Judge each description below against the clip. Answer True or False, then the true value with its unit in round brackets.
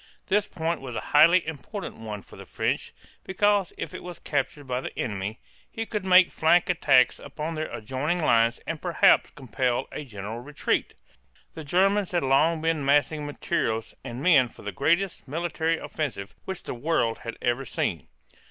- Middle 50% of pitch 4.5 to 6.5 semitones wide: True (5.5 semitones)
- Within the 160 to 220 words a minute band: True (170 wpm)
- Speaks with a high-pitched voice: False (150 Hz)